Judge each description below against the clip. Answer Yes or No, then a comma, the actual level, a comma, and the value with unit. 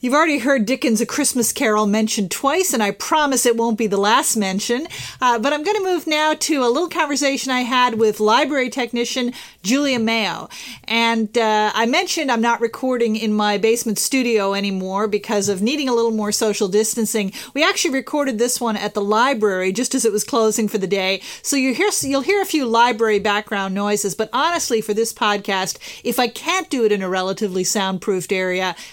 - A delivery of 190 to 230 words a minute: Yes, average, 200 wpm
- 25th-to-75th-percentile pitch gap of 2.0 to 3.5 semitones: No, average, 4.2 semitones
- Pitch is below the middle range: No, high, 230 Hz